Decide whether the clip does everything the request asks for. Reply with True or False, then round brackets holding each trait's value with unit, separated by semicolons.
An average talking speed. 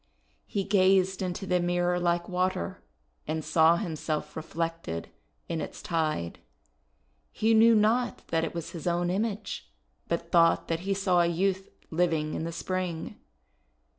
True (145 wpm)